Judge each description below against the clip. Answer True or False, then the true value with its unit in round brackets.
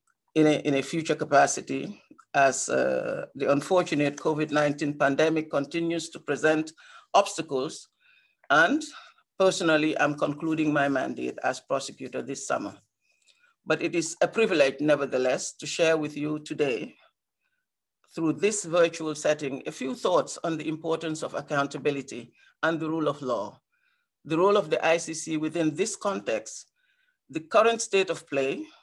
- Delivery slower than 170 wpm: True (140 wpm)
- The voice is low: False (160 Hz)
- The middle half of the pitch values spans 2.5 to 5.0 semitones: True (4.6 semitones)